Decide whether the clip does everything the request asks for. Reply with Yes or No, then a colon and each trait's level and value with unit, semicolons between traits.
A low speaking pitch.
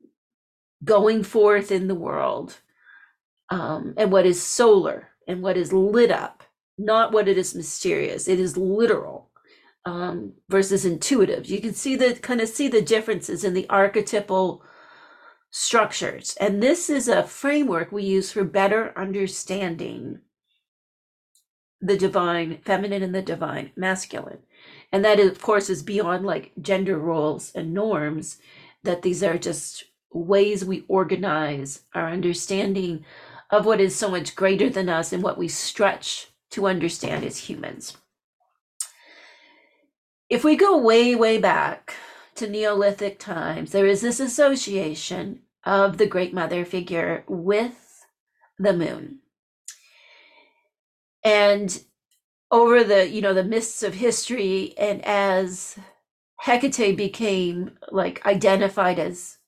No: high, 200 Hz